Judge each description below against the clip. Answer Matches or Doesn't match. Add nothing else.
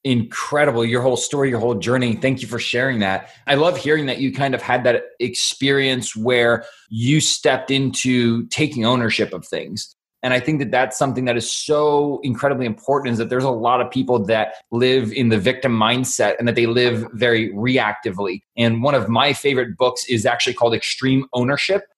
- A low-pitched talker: Matches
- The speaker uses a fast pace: Doesn't match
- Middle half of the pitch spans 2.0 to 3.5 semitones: Matches